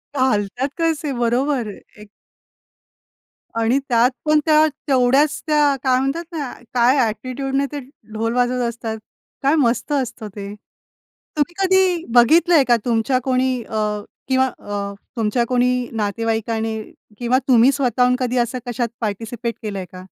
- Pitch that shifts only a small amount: No, average, 3.3 semitones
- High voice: Yes, very high, 250 Hz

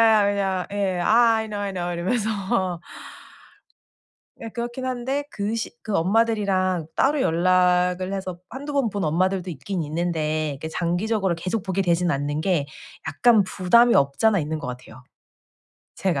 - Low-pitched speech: No, medium, 185 Hz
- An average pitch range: Yes, average, 4.4 semitones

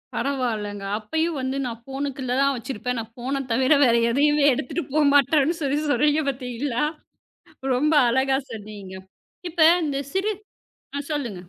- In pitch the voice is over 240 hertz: Yes, very high, 270 Hz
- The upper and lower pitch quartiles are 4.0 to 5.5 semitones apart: No, average, 3.6 semitones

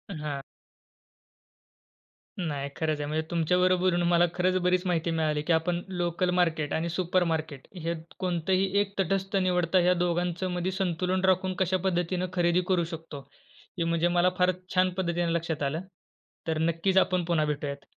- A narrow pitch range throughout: Yes, narrow, 2.1 semitones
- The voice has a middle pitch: Yes, medium, 175 Hz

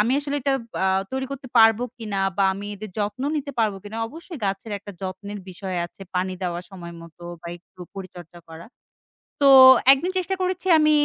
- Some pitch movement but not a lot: No, wide, 6.3 semitones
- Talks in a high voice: Yes, high, 205 Hz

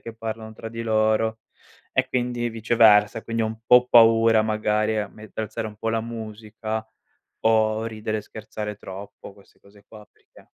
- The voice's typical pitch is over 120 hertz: No, low, 110 Hz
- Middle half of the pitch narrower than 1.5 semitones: Yes, narrow, 1.0 semitones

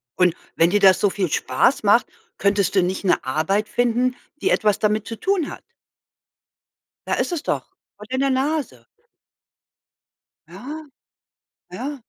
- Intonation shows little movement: No, wide, 5.5 semitones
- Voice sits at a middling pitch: No, high, 215 Hz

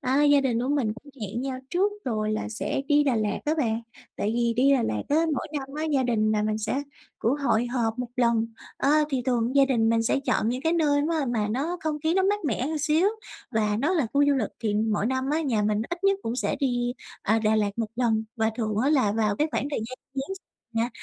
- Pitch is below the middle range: No, high, 245 Hz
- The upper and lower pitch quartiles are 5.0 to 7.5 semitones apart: No, average, 4.4 semitones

